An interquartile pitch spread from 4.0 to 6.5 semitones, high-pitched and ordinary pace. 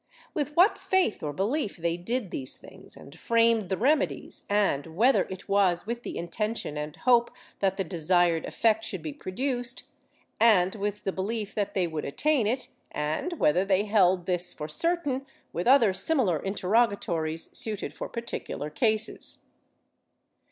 Yes: average, 5.2 semitones; high, 200 Hz; average, 160 wpm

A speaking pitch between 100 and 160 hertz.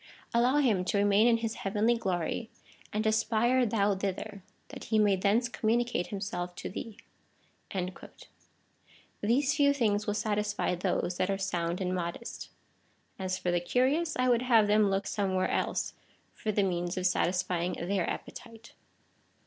No: high, 205 Hz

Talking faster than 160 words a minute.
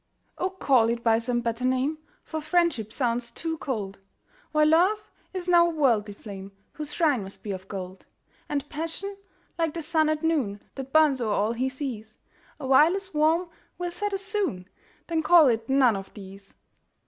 Yes: average, 180 wpm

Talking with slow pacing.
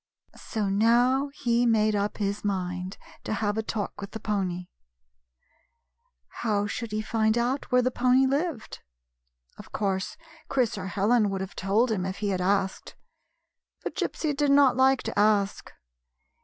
No: average, 155 wpm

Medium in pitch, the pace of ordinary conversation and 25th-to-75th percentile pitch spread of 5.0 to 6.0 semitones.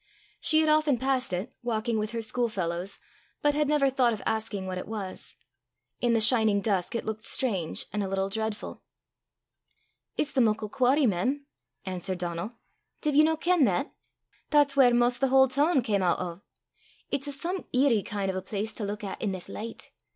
No: high, 225 Hz; average, 195 wpm; average, 5.3 semitones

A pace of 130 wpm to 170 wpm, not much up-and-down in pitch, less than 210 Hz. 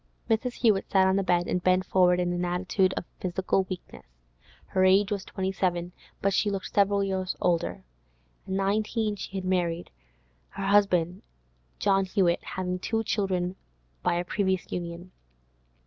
Yes: average, 160 wpm; narrow, 1.7 semitones; high, 190 Hz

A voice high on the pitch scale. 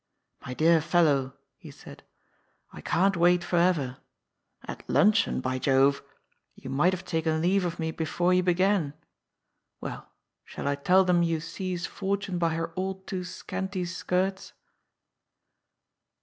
No: medium, 175 Hz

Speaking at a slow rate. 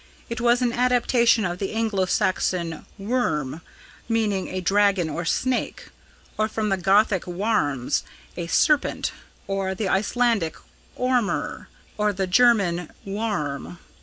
Yes: slow, 125 wpm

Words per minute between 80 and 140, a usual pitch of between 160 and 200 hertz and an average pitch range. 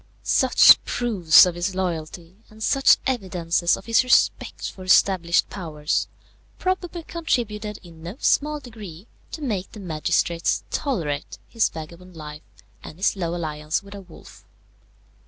Yes: slow, 135 wpm; medium, 185 Hz; average, 5.0 semitones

